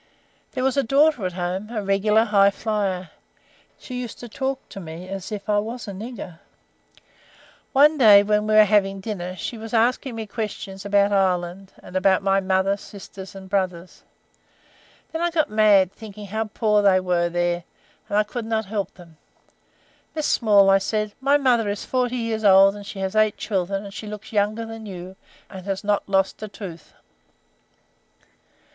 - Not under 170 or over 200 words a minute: Yes, average, 180 wpm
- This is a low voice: No, high, 205 Hz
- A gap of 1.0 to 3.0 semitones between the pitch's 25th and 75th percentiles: Yes, narrow, 2.4 semitones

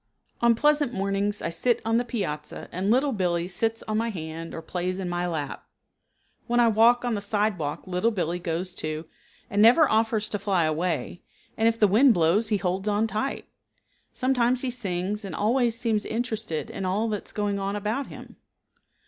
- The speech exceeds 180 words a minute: Yes, average, 190 wpm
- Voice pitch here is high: Yes, high, 205 Hz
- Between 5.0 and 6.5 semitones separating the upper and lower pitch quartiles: No, average, 4.3 semitones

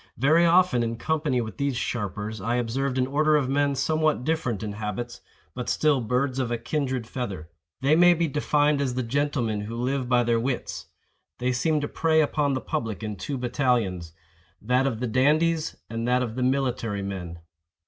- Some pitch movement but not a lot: Yes, average, 4.0 semitones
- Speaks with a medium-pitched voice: No, low, 125 Hz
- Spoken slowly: No, average, 185 wpm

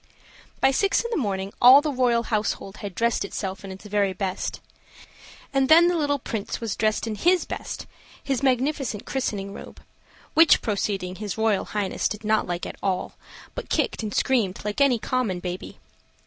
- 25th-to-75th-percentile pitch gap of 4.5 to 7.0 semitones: Yes, average, 5.2 semitones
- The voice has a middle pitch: No, high, 215 Hz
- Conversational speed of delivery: Yes, average, 175 wpm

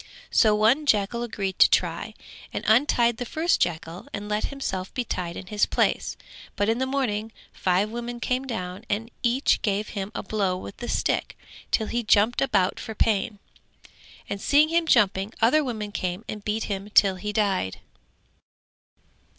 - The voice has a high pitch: Yes, high, 215 Hz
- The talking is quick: No, average, 170 wpm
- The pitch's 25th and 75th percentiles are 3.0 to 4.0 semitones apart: Yes, average, 3.5 semitones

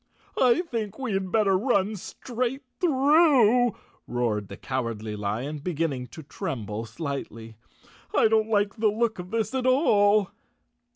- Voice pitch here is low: No, high, 205 Hz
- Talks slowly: Yes, slow, 130 wpm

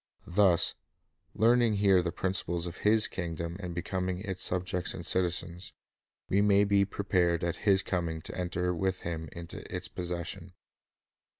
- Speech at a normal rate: Yes, average, 155 wpm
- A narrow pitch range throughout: Yes, narrow, 2.3 semitones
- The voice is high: No, very low, 90 Hz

